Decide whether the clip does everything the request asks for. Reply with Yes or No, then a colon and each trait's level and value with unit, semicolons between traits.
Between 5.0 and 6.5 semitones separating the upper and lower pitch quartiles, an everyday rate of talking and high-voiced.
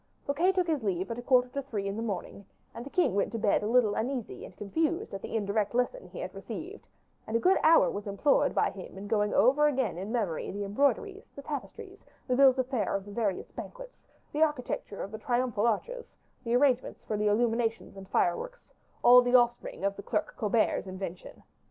No: wide, 5.5 semitones; fast, 215 wpm; high, 235 Hz